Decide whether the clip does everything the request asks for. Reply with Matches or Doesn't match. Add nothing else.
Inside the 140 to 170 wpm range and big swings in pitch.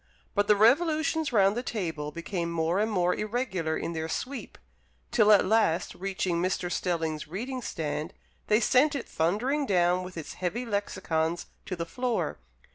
Matches